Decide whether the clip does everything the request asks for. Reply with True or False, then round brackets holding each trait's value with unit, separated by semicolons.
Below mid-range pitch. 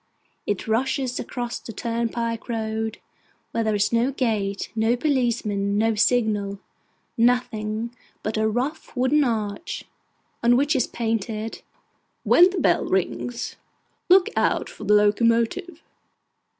False (230 Hz)